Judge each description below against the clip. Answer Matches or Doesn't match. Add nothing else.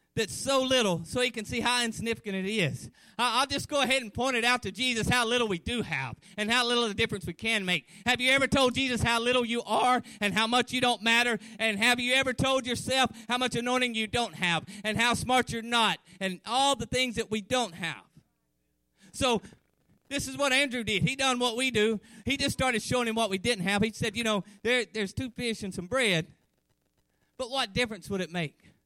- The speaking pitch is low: Doesn't match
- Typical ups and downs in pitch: Matches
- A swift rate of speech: Matches